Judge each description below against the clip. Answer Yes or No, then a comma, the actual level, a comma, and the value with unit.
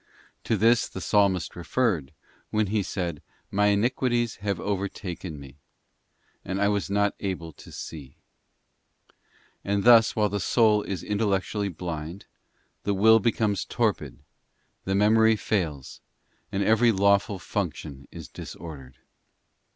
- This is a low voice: Yes, low, 100 Hz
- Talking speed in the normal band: No, slow, 125 wpm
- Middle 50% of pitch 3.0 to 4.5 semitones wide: Yes, average, 3.4 semitones